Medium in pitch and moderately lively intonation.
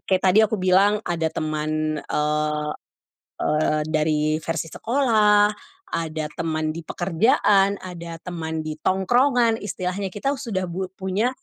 Yes: medium, 180 Hz; average, 4.8 semitones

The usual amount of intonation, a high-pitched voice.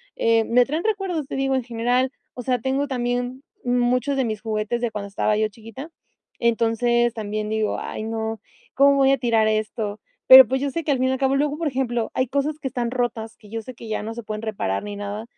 Yes: average, 3.2 semitones; high, 240 Hz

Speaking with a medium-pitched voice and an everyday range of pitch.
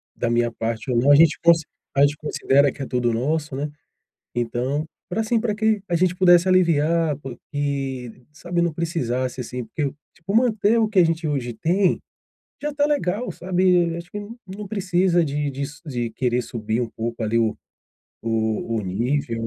No: medium, 145 Hz; wide, 6.5 semitones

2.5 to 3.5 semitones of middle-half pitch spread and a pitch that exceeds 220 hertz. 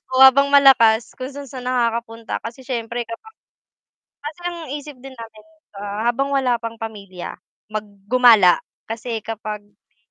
Yes: average, 3.2 semitones; high, 235 Hz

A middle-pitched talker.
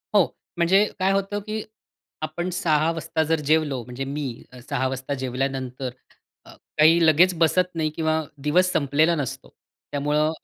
Yes: medium, 155 Hz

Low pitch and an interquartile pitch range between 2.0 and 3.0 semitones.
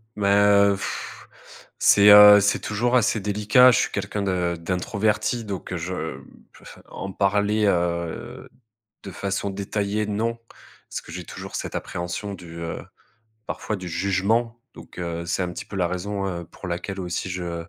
Yes: low, 100 Hz; average, 2.7 semitones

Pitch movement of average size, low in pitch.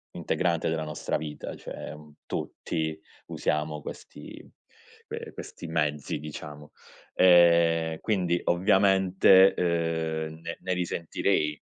No: narrow, 2.3 semitones; very low, 80 Hz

